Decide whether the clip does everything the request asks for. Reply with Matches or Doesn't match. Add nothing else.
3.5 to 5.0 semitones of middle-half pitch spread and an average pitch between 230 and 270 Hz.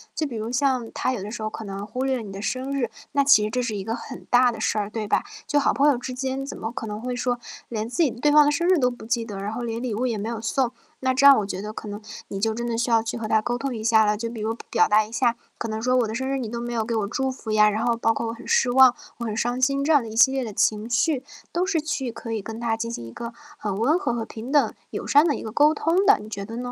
Doesn't match